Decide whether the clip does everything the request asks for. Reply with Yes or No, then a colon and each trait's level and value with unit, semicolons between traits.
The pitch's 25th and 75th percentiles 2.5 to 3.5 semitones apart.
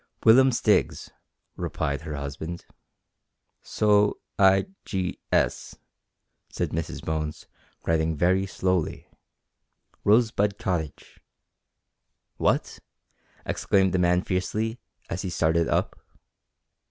No: average, 4.1 semitones